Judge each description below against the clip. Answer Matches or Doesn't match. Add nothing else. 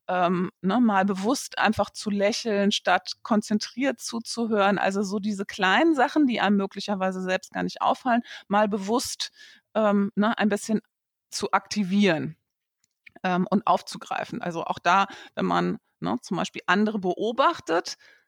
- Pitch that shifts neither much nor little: Matches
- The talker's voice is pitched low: Doesn't match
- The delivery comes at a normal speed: Matches